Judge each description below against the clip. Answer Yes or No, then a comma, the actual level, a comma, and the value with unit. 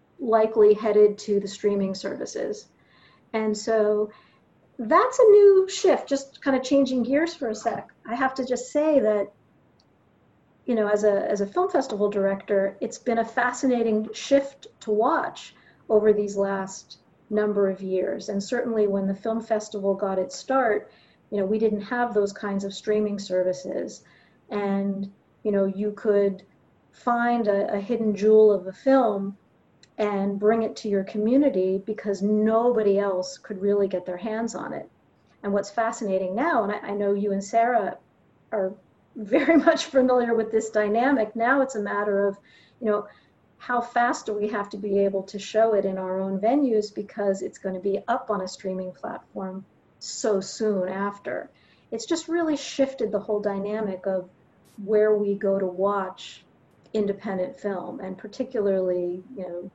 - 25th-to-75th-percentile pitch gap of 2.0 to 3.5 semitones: Yes, average, 3.0 semitones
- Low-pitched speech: No, high, 210 Hz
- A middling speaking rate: Yes, average, 170 wpm